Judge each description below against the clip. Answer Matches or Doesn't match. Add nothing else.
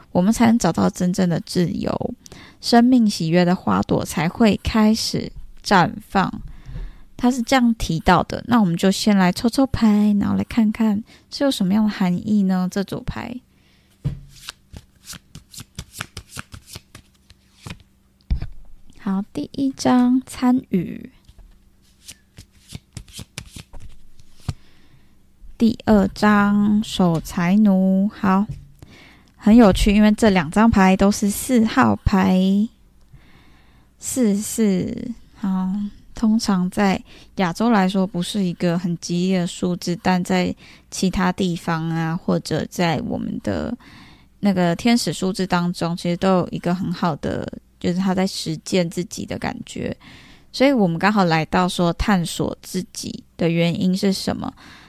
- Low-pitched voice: Doesn't match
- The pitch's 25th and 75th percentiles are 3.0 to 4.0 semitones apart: Matches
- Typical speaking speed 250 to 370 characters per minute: Doesn't match